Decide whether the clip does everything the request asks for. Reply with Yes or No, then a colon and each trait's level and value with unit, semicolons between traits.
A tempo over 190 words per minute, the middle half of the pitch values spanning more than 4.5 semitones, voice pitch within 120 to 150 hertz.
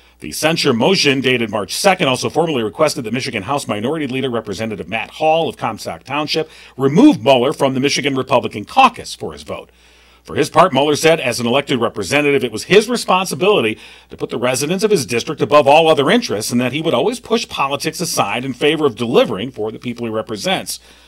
Yes: average, 200 wpm; wide, 5.4 semitones; medium, 140 Hz